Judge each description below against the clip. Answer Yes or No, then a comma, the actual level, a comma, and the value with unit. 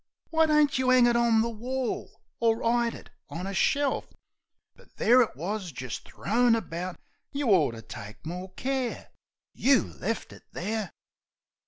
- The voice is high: Yes, high, 230 Hz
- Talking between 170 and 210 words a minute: No, average, 160 wpm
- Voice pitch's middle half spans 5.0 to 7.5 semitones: Yes, wide, 5.6 semitones